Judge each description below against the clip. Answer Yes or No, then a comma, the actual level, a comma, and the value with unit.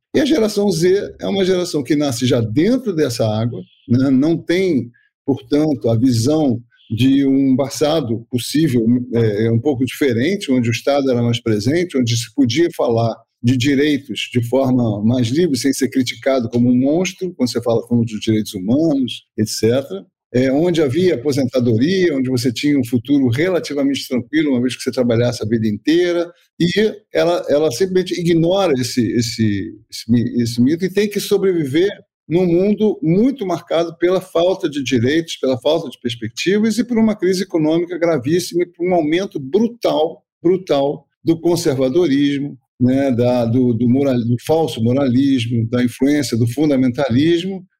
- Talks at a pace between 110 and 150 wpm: No, average, 160 wpm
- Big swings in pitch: Yes, wide, 6.1 semitones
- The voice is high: No, medium, 140 Hz